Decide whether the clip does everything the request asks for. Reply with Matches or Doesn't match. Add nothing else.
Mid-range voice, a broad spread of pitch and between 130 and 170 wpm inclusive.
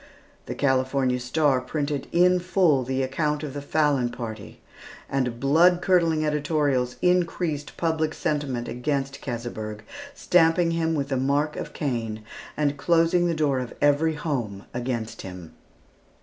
Doesn't match